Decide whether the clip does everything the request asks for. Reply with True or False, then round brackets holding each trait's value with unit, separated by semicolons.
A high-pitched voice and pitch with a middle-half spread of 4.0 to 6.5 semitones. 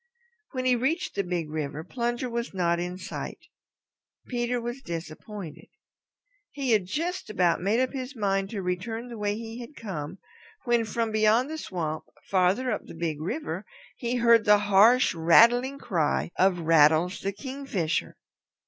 True (210 Hz; 5.4 semitones)